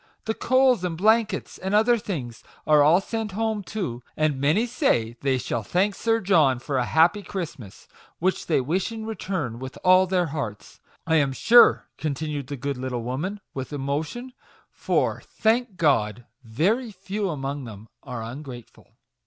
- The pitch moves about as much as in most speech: No, wide, 7.7 semitones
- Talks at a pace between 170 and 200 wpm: Yes, average, 175 wpm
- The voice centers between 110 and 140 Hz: No, medium, 160 Hz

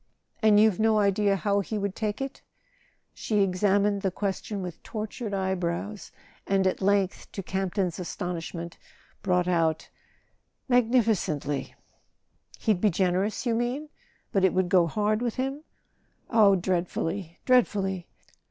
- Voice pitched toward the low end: No, high, 200 Hz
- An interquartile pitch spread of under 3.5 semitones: Yes, average, 2.9 semitones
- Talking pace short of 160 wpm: Yes, average, 145 wpm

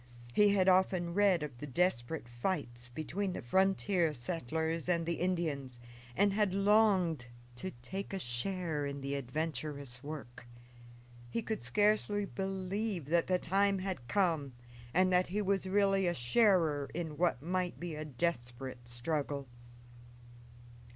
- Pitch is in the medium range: Yes, medium, 170 Hz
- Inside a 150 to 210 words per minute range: No, average, 140 wpm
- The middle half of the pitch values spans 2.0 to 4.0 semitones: No, average, 5.3 semitones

